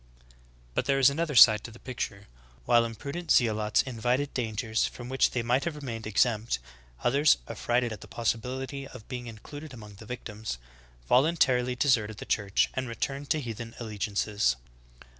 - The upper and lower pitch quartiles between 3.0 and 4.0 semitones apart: Yes, average, 3.4 semitones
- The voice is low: Yes, low, 120 Hz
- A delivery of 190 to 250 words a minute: No, average, 175 wpm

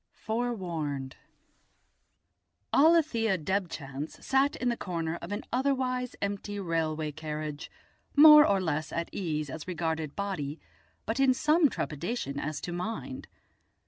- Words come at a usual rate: No, slow, 120 wpm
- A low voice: No, medium, 185 Hz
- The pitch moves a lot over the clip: Yes, wide, 7.8 semitones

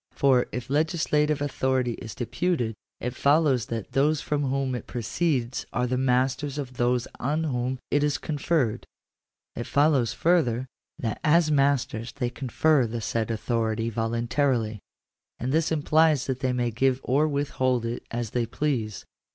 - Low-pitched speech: Yes, low, 130 Hz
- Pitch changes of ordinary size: Yes, average, 3.6 semitones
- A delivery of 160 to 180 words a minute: No, average, 150 wpm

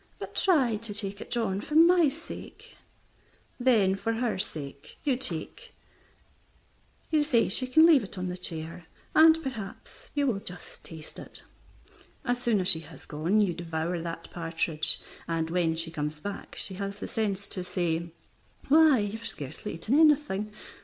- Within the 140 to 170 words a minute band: Yes, average, 160 wpm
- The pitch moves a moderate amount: No, wide, 7.1 semitones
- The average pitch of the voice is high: Yes, high, 200 Hz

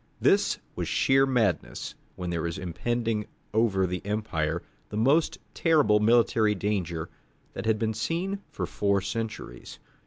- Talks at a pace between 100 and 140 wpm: Yes, slow, 135 wpm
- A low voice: Yes, low, 105 Hz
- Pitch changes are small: No, average, 4.3 semitones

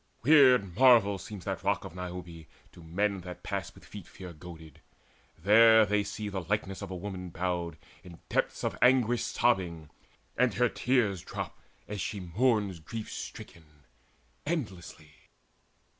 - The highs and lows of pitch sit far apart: No, average, 4.4 semitones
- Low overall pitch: Yes, very low, 95 Hz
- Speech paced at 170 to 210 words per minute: No, average, 145 wpm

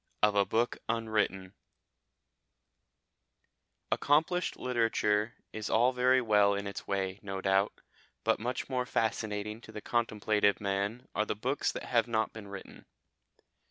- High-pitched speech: No, low, 110 Hz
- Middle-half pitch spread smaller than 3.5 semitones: Yes, average, 2.8 semitones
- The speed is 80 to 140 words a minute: Yes, slow, 135 wpm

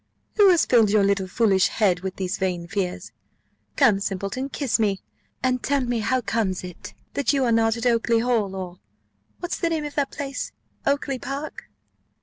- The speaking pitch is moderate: No, high, 225 Hz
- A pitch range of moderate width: No, wide, 5.8 semitones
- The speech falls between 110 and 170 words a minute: No, average, 180 wpm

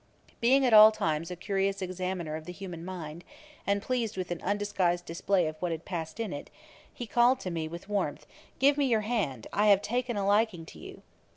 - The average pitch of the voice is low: No, high, 190 Hz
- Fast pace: Yes, fast, 210 wpm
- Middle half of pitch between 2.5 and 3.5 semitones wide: No, average, 4.2 semitones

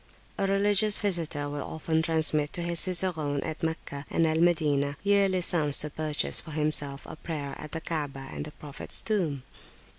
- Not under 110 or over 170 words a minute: No, average, 180 wpm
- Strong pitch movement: No, average, 3.0 semitones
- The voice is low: No, medium, 160 Hz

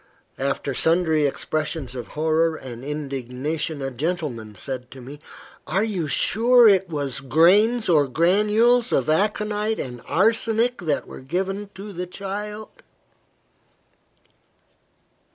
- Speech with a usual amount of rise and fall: No, wide, 7.0 semitones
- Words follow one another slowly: Yes, slow, 115 wpm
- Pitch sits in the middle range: Yes, medium, 165 Hz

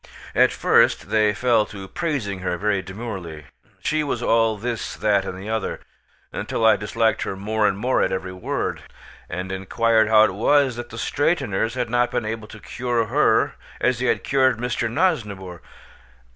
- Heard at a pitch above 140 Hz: No, low, 110 Hz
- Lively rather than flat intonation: No, average, 3.6 semitones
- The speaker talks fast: No, average, 175 wpm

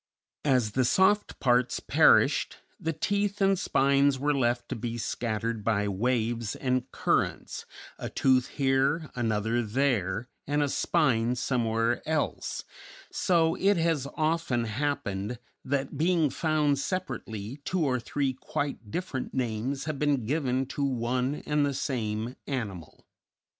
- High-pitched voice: No, low, 130 Hz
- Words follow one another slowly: Yes, slow, 130 wpm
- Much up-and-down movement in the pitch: No, average, 4.0 semitones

